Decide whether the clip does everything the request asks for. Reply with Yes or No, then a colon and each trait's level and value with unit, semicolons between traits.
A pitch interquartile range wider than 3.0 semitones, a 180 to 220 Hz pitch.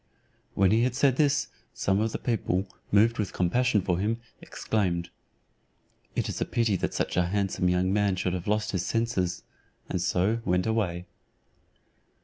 No: average, 3.8 semitones; low, 100 Hz